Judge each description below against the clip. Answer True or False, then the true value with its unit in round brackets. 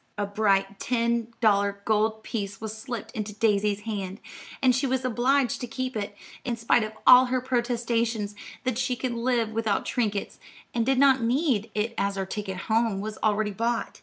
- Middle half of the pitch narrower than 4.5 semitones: True (2.8 semitones)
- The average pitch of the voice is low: False (225 Hz)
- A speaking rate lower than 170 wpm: False (180 wpm)